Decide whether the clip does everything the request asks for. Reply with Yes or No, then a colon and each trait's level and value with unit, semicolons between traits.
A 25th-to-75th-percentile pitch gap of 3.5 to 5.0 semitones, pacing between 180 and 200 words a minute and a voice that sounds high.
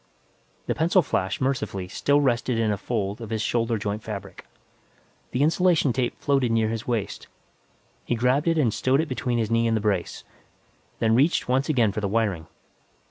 No: average, 3.9 semitones; average, 185 wpm; low, 115 Hz